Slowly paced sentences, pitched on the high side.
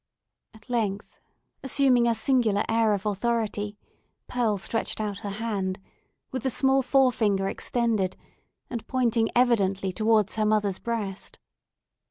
Yes: slow, 125 wpm; high, 220 Hz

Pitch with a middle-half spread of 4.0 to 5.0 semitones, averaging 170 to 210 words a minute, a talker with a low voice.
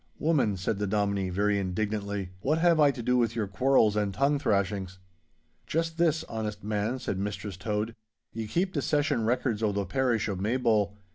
Yes: average, 4.5 semitones; average, 185 wpm; low, 110 Hz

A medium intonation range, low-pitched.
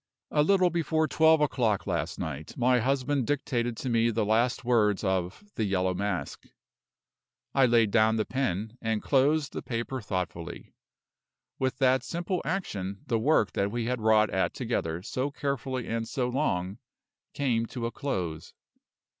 Yes: average, 5.0 semitones; low, 115 Hz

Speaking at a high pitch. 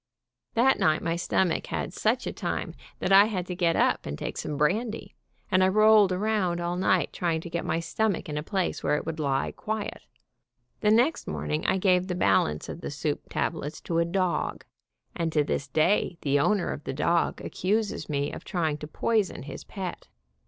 No: medium, 175 Hz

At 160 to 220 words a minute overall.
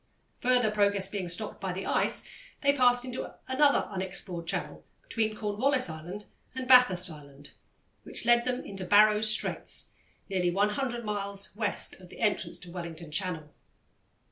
No: average, 145 wpm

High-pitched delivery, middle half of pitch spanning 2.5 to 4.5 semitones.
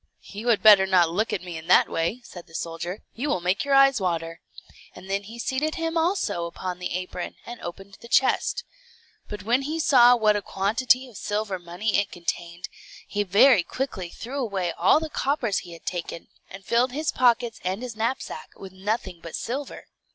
No: high, 205 Hz; wide, 5.5 semitones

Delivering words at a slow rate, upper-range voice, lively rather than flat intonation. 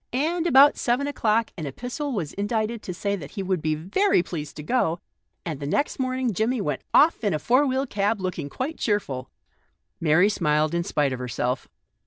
No: average, 195 wpm; high, 200 Hz; wide, 8.5 semitones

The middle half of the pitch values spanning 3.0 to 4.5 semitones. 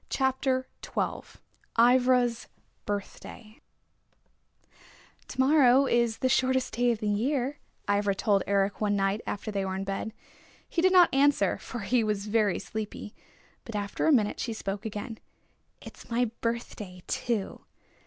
Yes: average, 4.0 semitones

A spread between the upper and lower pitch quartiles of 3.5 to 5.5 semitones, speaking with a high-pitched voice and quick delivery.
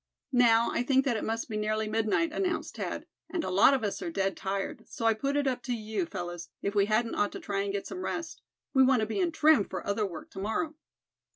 Yes: average, 5.1 semitones; high, 220 Hz; fast, 255 wpm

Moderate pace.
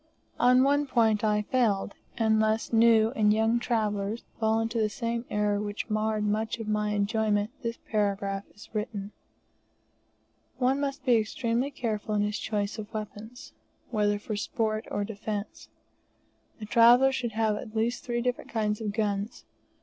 Yes: average, 155 wpm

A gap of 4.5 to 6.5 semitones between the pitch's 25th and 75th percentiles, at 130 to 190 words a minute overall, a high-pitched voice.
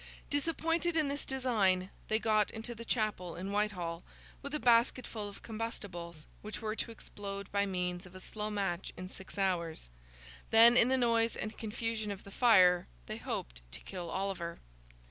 No: average, 4.0 semitones; average, 170 wpm; high, 210 Hz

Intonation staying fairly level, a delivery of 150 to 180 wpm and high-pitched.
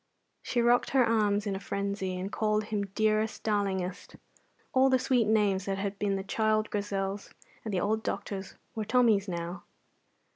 Yes: narrow, 2.0 semitones; average, 170 wpm; high, 205 Hz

